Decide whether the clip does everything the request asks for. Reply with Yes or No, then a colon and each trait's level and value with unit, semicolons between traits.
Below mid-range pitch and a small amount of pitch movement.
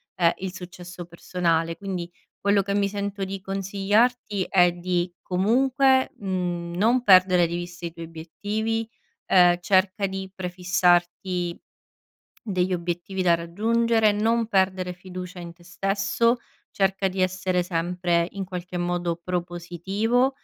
No: medium, 185 Hz; narrow, 2.3 semitones